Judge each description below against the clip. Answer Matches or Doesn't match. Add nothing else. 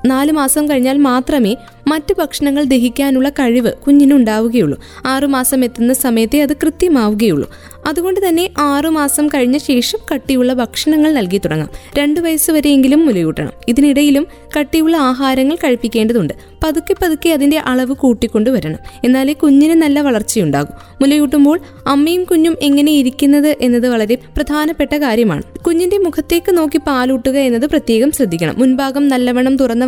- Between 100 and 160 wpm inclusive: Matches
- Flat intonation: Doesn't match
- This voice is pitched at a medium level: Doesn't match